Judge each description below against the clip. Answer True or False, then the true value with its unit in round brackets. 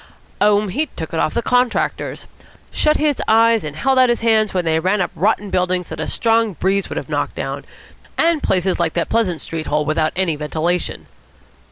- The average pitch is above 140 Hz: True (190 Hz)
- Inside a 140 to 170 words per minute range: False (200 wpm)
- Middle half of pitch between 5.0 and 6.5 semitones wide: True (5.6 semitones)